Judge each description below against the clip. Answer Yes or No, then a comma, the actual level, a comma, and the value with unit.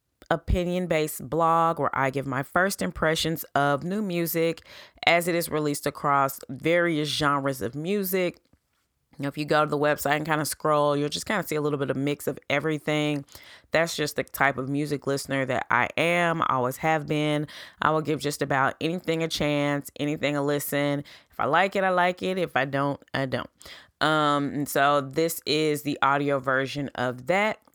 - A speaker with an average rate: Yes, average, 195 wpm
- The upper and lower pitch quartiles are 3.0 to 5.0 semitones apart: No, narrow, 2.6 semitones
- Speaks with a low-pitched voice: No, medium, 150 Hz